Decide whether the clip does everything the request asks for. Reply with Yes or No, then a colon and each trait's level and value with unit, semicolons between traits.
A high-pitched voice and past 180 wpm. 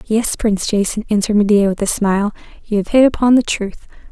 Yes: high, 210 Hz; fast, 205 wpm